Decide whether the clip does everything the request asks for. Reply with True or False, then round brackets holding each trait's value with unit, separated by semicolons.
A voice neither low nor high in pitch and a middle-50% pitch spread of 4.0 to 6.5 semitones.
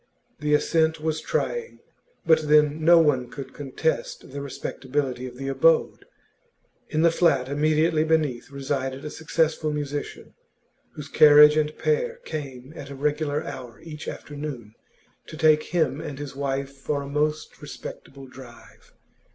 False (150 Hz; 2.4 semitones)